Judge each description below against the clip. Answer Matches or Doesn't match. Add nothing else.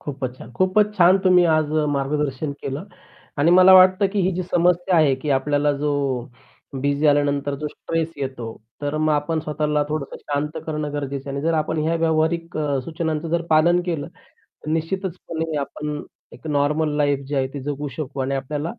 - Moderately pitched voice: Matches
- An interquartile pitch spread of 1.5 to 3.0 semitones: Matches